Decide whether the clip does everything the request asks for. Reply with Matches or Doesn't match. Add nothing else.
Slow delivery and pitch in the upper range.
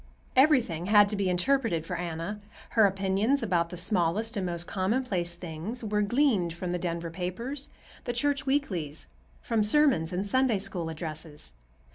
Doesn't match